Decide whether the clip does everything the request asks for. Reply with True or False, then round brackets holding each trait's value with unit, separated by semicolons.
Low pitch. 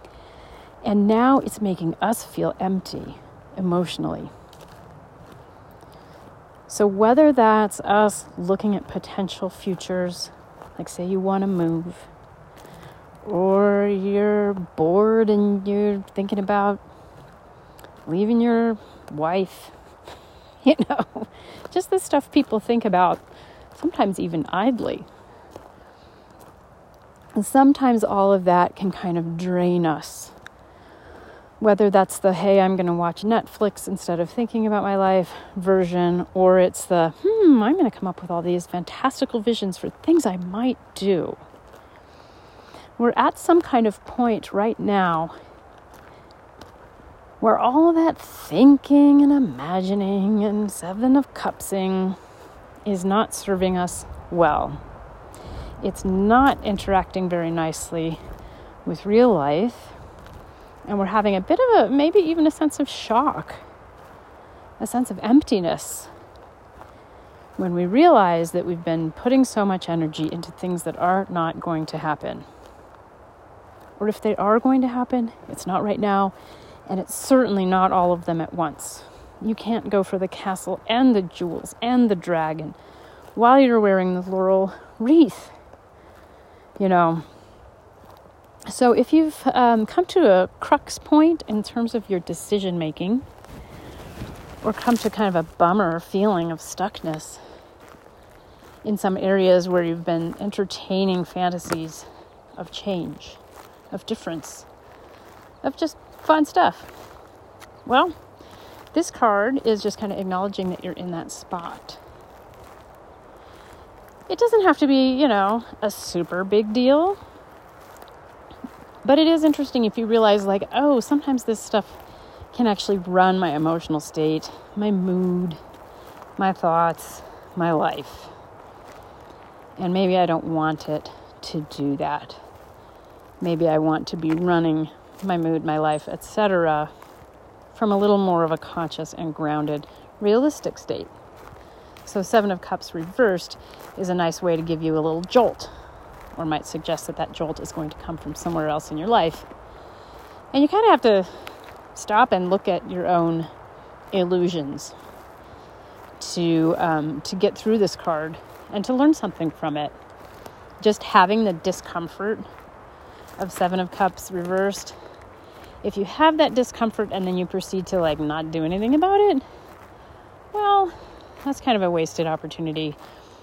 False (195 Hz)